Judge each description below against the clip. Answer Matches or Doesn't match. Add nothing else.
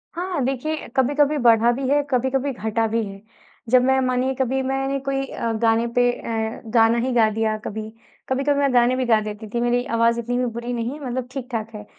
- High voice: Matches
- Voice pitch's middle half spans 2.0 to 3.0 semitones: Matches